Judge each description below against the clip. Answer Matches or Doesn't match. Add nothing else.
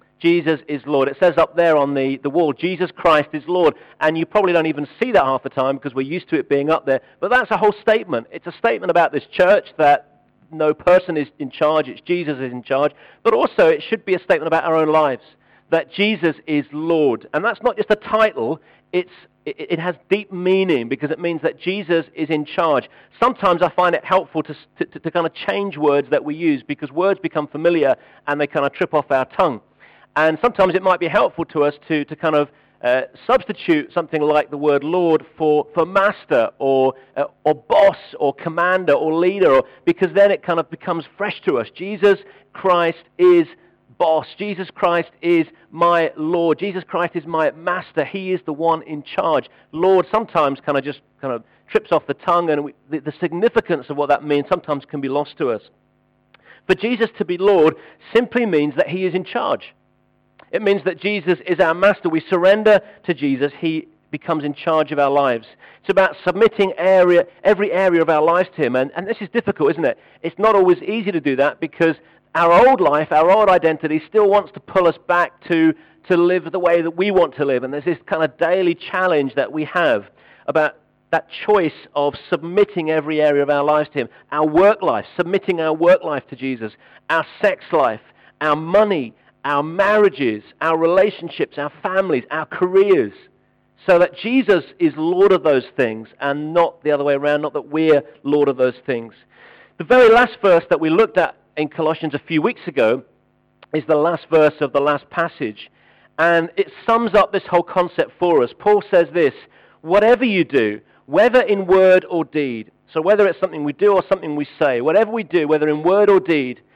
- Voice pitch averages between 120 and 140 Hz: Doesn't match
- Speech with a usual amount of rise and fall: Matches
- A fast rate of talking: Matches